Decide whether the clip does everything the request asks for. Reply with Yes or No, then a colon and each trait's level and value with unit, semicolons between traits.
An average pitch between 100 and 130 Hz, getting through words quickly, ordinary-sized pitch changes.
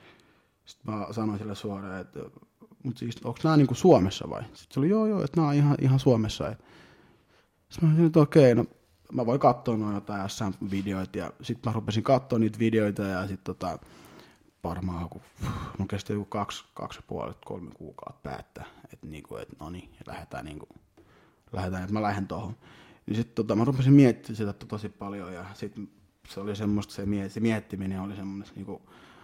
Yes: low, 105 Hz; fast, 195 wpm; average, 3.3 semitones